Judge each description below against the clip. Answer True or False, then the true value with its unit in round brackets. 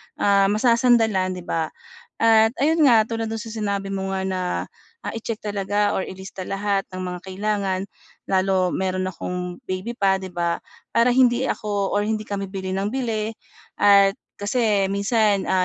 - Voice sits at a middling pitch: False (200 Hz)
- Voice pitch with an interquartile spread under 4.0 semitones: True (2.7 semitones)